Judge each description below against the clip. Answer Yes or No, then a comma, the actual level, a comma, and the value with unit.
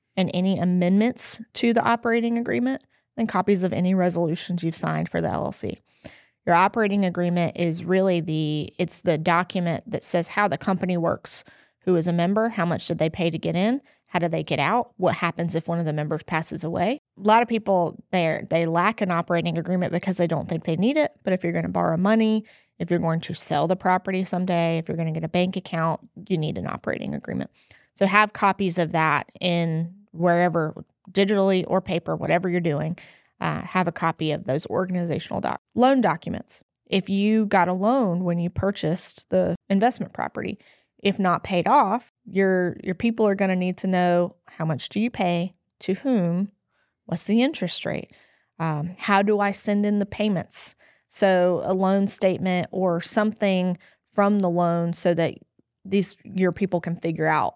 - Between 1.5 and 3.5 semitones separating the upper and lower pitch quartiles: Yes, average, 3.0 semitones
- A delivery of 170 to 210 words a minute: Yes, average, 195 wpm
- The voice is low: No, medium, 185 Hz